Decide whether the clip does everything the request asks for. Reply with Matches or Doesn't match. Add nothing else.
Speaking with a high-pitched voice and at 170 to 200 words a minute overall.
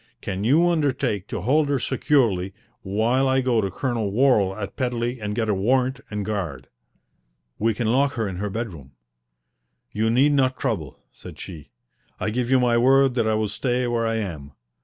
Doesn't match